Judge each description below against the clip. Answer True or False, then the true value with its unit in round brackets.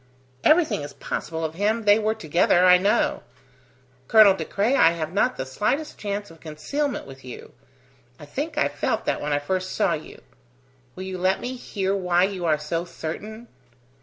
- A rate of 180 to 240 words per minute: True (185 wpm)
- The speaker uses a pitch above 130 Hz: True (185 Hz)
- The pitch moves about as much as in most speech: True (4.8 semitones)